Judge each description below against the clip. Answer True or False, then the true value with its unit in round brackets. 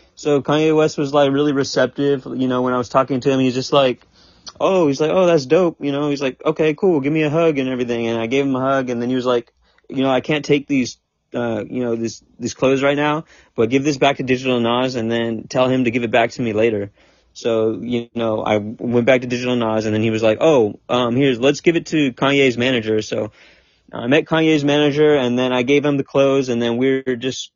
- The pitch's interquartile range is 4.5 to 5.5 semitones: False (3.2 semitones)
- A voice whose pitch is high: False (130 Hz)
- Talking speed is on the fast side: True (260 wpm)